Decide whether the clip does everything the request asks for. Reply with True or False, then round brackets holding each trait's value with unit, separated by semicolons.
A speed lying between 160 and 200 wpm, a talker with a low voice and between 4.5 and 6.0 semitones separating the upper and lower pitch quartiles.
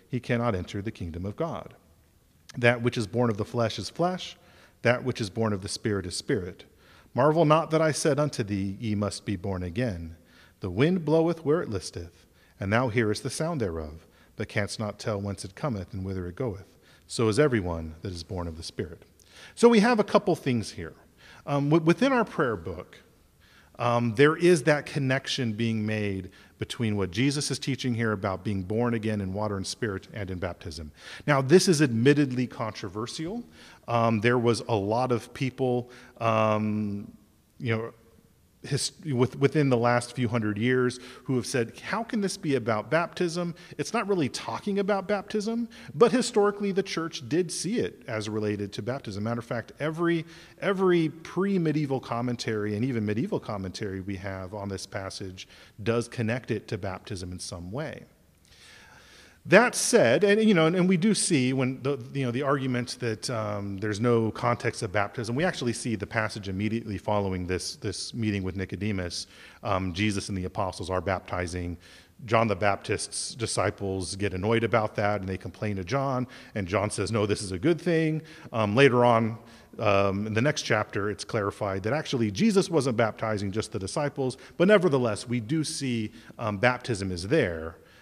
True (180 wpm; 115 Hz; 5.5 semitones)